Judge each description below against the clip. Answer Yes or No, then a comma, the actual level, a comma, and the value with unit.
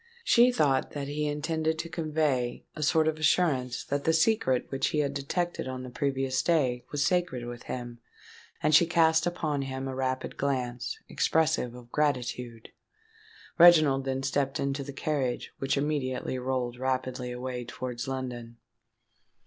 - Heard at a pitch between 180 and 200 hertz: No, low, 135 Hz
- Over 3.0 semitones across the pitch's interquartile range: Yes, average, 3.4 semitones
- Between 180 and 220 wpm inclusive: No, average, 155 wpm